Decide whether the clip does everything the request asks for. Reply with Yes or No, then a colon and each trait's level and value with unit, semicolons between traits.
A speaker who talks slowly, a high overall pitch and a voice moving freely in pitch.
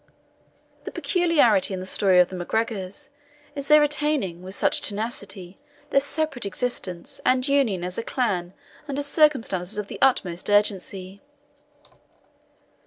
Yes: slow, 130 wpm; high, 205 Hz; wide, 6.9 semitones